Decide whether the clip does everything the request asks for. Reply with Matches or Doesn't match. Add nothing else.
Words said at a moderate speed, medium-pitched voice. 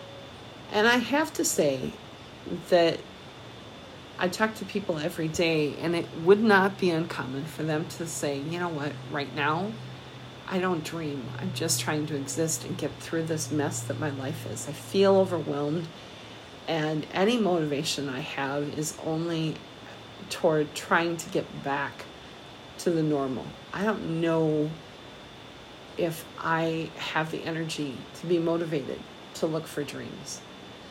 Matches